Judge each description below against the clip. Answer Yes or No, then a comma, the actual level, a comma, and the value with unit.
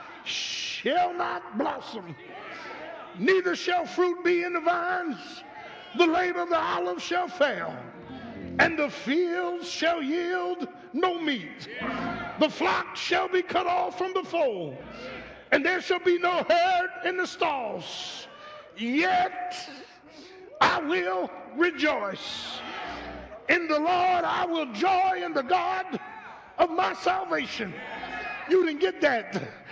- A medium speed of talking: No, slow, 125 wpm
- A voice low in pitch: No, very high, 350 Hz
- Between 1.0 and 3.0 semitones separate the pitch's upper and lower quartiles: Yes, average, 2.7 semitones